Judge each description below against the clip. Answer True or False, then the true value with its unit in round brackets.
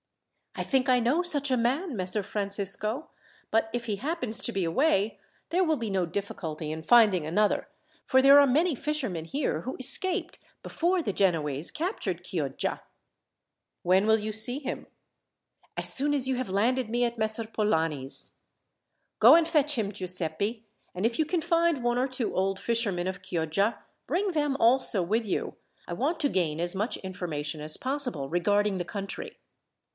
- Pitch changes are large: True (6.6 semitones)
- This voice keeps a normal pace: True (170 wpm)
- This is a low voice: False (220 Hz)